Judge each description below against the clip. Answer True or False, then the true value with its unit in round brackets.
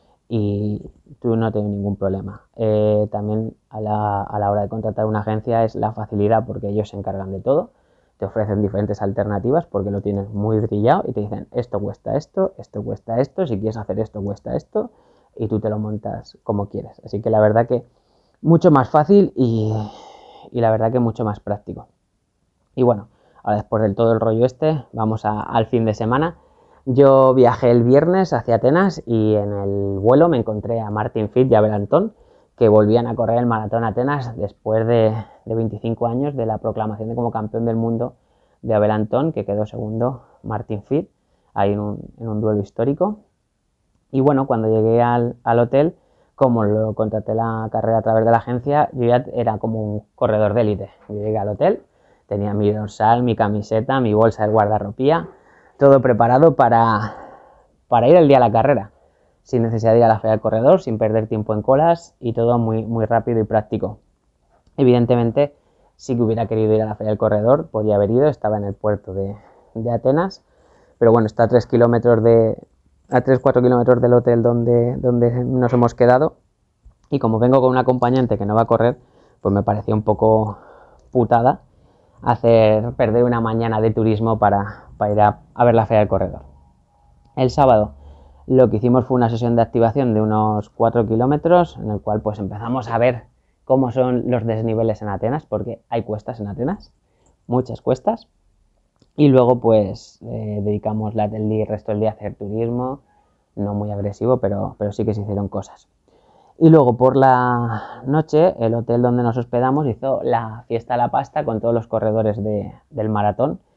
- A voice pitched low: True (115 Hz)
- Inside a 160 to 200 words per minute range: True (190 wpm)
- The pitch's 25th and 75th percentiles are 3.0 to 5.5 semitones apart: False (2.6 semitones)